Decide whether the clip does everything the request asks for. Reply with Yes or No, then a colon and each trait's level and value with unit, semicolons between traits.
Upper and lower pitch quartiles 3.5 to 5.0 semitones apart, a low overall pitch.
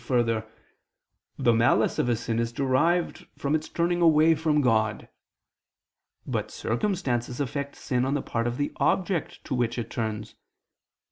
Yes: average, 4.6 semitones; low, 125 Hz